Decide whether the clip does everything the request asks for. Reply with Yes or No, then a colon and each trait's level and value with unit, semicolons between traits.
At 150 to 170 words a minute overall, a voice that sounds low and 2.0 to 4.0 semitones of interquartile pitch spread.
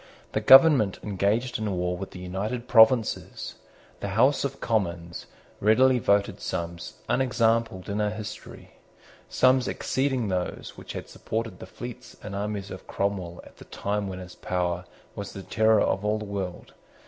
Yes: average, 160 wpm; low, 105 Hz; average, 3.6 semitones